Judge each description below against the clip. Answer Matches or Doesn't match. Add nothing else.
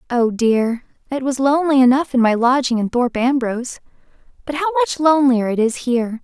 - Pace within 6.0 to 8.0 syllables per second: Matches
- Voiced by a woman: Matches